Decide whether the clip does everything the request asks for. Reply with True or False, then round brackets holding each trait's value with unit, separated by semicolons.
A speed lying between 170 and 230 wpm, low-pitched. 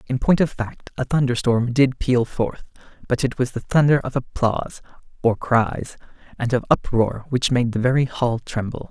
True (180 wpm; 125 Hz)